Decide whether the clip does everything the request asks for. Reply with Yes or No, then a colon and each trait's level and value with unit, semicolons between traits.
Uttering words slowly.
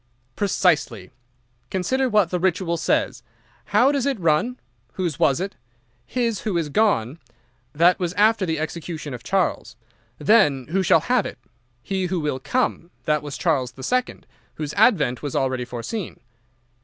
No: average, 155 wpm